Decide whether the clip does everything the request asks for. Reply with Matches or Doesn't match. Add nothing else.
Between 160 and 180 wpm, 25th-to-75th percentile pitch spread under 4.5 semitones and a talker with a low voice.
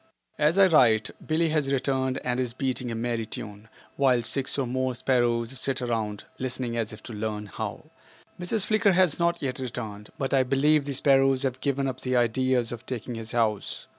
Doesn't match